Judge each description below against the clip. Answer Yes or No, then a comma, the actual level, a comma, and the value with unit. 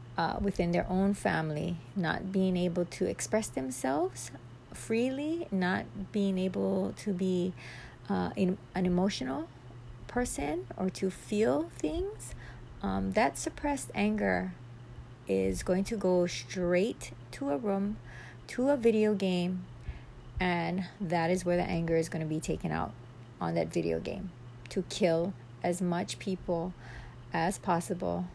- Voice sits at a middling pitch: Yes, medium, 175 Hz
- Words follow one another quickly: No, average, 140 wpm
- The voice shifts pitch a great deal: Yes, wide, 7.7 semitones